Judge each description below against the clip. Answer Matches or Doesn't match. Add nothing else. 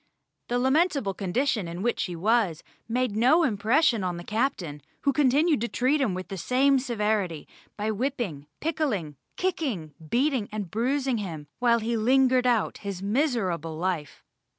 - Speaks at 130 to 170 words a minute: Matches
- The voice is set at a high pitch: Matches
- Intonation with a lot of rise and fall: Matches